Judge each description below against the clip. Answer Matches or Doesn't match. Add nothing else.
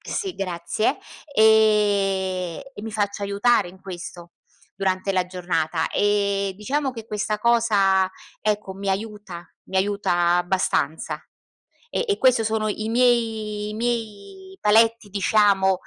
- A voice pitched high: Matches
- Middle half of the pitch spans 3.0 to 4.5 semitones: Doesn't match